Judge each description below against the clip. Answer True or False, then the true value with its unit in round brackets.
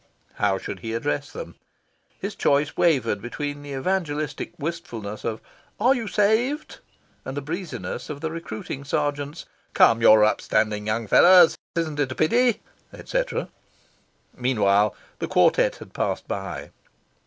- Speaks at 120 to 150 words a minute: True (140 wpm)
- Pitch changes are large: True (7.3 semitones)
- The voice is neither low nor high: True (145 Hz)